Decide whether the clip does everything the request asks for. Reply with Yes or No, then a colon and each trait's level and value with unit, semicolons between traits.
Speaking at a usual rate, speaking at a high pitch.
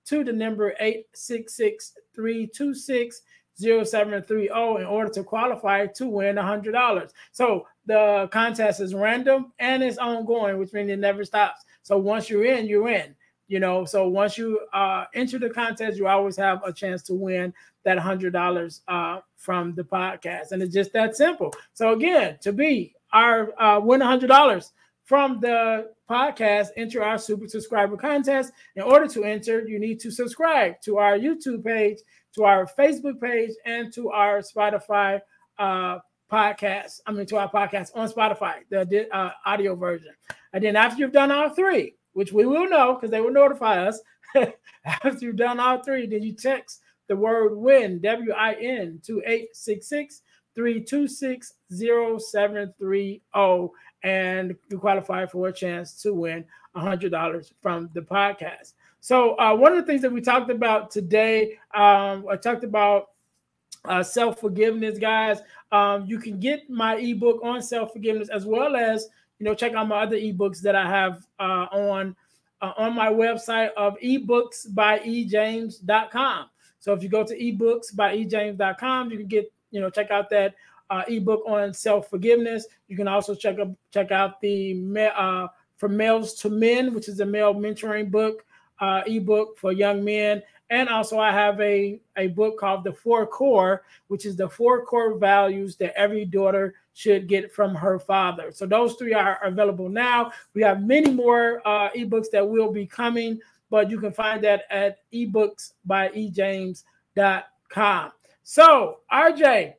Yes: average, 165 wpm; high, 215 Hz